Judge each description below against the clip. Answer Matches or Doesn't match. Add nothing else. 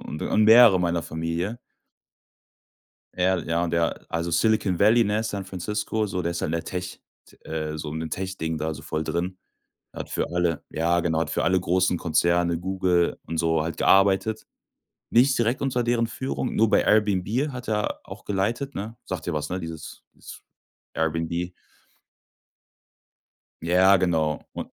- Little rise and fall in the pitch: Doesn't match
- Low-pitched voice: Matches